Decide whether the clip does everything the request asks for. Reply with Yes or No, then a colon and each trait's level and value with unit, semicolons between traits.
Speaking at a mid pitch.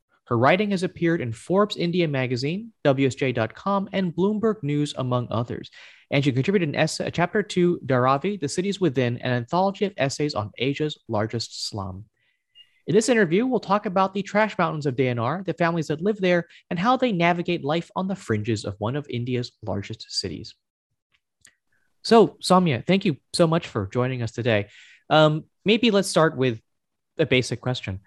Yes: medium, 160 Hz